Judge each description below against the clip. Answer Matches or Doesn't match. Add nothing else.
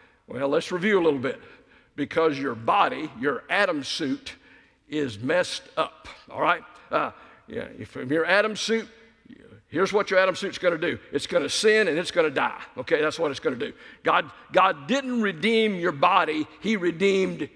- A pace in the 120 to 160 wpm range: Doesn't match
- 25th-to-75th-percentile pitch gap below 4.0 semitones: Doesn't match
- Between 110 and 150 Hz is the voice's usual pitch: Doesn't match